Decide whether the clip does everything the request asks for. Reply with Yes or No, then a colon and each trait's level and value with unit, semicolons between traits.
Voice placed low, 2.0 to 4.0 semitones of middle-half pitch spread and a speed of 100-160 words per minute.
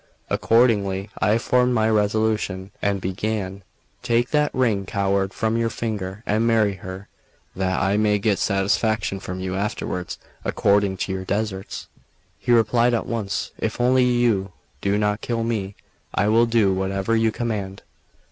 Yes: low, 105 Hz; average, 2.9 semitones; average, 150 wpm